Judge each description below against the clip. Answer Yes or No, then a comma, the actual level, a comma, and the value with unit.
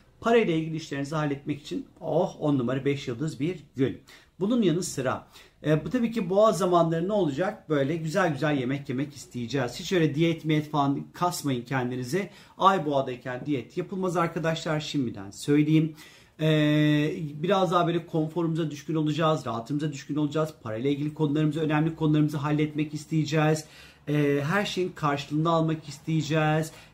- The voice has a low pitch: No, medium, 155 Hz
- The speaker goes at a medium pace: No, fast, 145 wpm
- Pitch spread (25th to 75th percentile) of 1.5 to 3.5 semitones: Yes, narrow, 2.5 semitones